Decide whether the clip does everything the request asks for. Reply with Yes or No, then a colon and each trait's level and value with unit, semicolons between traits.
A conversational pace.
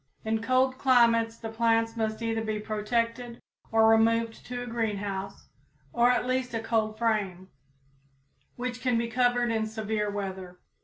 Yes: average, 150 wpm